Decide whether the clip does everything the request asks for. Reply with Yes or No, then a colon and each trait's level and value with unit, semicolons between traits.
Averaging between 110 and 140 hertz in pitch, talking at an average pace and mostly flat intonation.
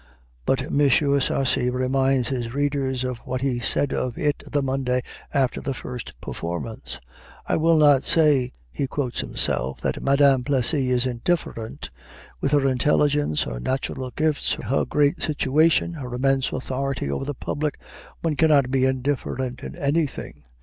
Yes: low, 135 Hz; average, 150 wpm; narrow, 2.3 semitones